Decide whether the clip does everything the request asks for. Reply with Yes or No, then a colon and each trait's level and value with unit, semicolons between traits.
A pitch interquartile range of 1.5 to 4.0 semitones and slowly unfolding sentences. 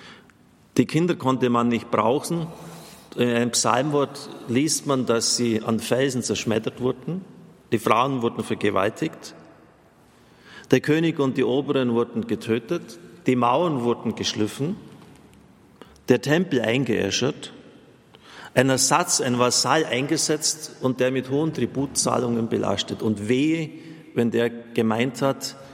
Yes: average, 3.6 semitones; slow, 120 wpm